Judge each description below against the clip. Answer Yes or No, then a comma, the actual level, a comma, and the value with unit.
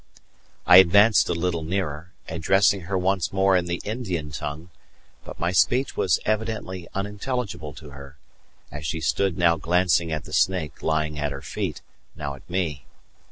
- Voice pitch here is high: No, very low, 85 Hz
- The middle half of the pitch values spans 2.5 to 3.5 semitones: No, average, 3.9 semitones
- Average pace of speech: Yes, average, 160 wpm